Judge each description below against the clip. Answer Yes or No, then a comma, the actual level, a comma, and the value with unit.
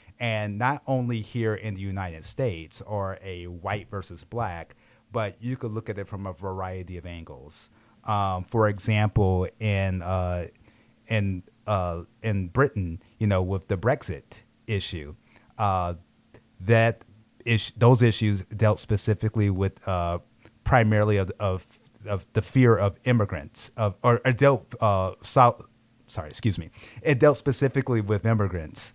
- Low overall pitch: Yes, low, 105 Hz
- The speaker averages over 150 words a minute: No, average, 145 wpm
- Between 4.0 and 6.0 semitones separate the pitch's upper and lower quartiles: No, average, 3.4 semitones